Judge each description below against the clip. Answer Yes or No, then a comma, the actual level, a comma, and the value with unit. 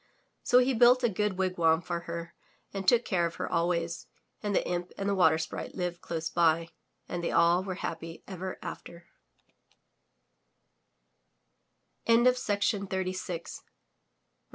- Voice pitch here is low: No, medium, 175 Hz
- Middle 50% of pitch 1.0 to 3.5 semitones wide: Yes, narrow, 2.5 semitones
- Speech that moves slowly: Yes, slow, 130 wpm